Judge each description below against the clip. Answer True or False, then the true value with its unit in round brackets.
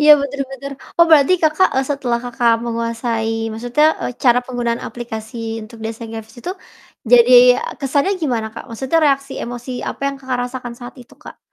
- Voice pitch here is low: False (245 Hz)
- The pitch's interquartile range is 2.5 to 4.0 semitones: True (2.9 semitones)